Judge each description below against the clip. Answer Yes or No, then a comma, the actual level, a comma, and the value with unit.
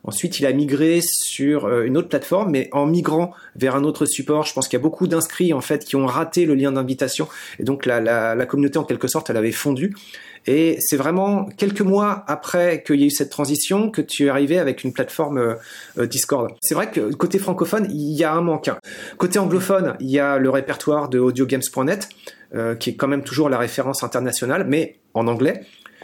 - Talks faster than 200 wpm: Yes, fast, 220 wpm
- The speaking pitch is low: No, medium, 150 Hz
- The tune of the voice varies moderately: Yes, average, 4.3 semitones